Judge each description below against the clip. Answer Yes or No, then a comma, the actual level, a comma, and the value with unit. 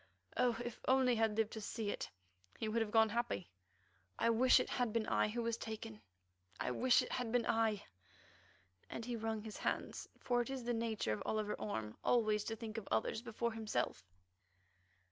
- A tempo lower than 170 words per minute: No, average, 195 wpm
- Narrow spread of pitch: Yes, narrow, 1.9 semitones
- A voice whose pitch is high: Yes, high, 225 Hz